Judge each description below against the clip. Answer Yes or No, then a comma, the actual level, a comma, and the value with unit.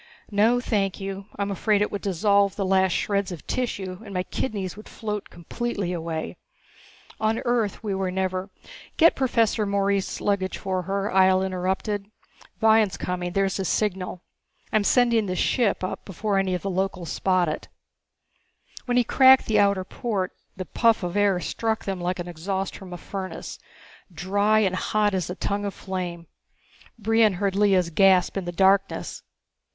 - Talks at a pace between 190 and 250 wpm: No, average, 165 wpm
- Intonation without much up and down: Yes, narrow, 2.1 semitones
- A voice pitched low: No, high, 195 Hz